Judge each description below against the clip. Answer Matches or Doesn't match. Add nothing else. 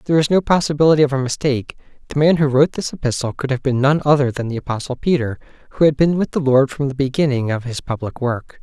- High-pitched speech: Doesn't match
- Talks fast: Matches